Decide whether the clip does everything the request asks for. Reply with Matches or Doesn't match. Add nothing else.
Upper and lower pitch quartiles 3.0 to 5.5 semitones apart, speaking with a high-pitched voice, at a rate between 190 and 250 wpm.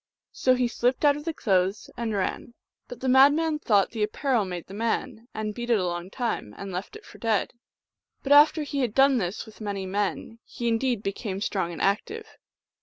Matches